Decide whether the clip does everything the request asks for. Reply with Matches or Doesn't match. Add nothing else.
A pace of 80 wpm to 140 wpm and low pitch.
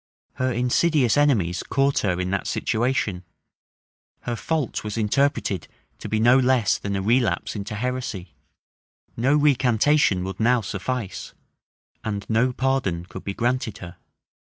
Matches